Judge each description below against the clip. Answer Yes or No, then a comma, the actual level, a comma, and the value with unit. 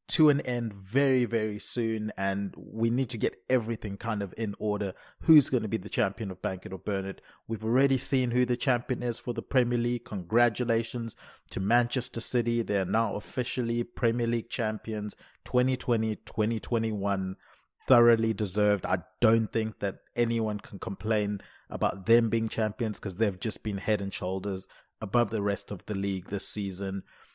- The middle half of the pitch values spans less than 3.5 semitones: Yes, average, 2.9 semitones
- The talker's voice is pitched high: No, low, 110 Hz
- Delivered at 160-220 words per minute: Yes, average, 170 wpm